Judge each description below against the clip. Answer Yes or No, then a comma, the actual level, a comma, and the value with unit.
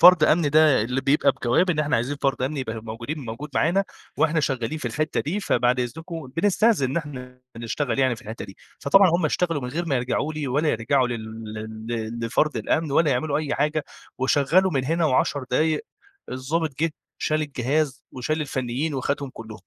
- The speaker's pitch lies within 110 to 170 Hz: Yes, medium, 140 Hz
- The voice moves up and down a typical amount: Yes, average, 3.9 semitones